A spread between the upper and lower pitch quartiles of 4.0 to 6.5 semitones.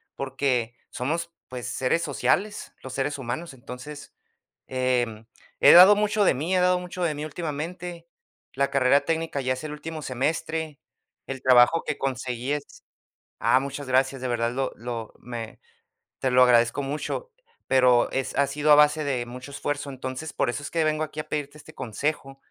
No: average, 3.5 semitones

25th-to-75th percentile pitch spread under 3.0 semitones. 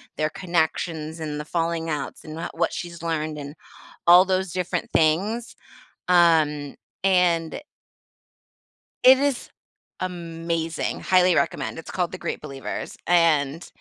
Yes: narrow, 2.4 semitones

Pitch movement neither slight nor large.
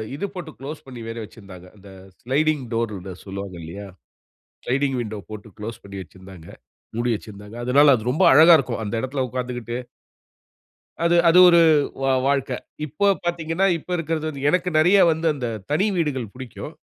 No: wide, 6.6 semitones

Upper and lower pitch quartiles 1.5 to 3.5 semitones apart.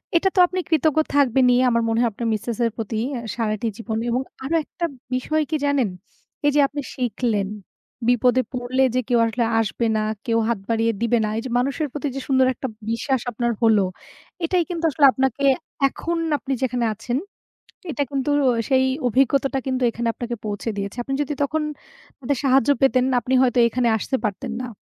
Yes: average, 3.0 semitones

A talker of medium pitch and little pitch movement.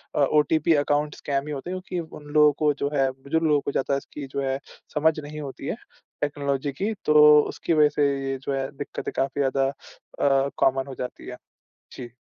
Yes: medium, 145 Hz; narrow, 1.8 semitones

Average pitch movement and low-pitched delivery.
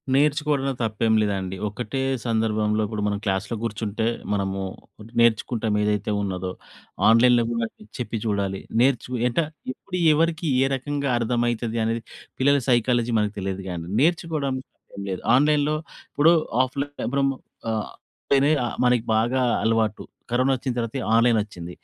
Yes: average, 4.2 semitones; low, 115 Hz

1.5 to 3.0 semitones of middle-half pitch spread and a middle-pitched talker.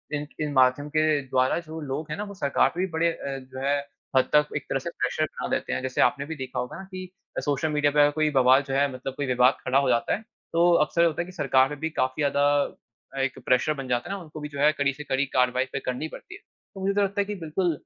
No: average, 3.4 semitones; medium, 145 Hz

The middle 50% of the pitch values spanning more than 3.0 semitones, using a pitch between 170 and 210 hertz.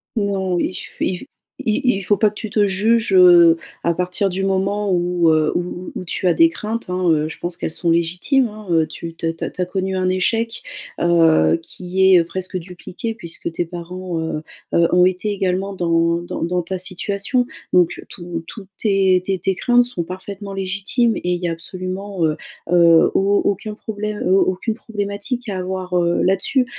No: average, 2.7 semitones; medium, 185 Hz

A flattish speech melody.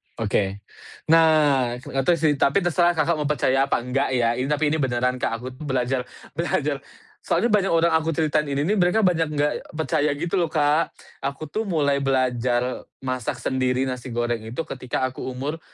No: average, 4.0 semitones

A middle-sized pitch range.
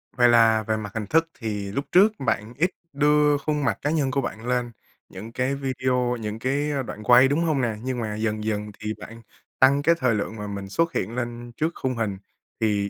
Yes: average, 4.2 semitones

